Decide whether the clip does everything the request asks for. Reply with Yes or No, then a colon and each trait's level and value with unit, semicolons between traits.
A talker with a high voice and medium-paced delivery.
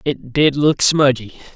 No: medium, 140 Hz; average, 155 wpm